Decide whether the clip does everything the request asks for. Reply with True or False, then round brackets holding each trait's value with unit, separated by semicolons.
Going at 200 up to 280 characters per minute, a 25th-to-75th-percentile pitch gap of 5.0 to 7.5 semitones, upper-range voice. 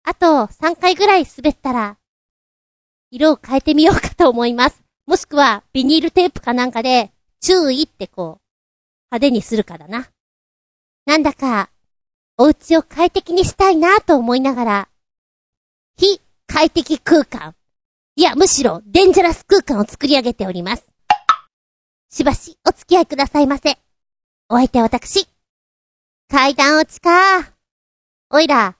True (270 characters per minute; 5.8 semitones; 290 Hz)